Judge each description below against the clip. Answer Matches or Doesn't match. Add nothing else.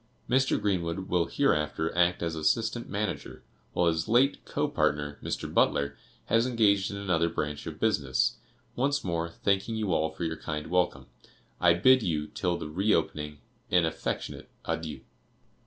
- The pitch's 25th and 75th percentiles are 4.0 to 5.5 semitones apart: Matches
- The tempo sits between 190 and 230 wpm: Doesn't match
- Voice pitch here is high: Doesn't match